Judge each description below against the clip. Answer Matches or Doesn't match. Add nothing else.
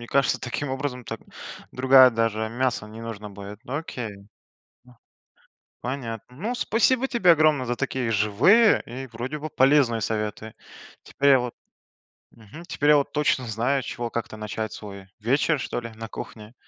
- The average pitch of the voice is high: Doesn't match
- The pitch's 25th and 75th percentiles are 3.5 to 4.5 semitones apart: Matches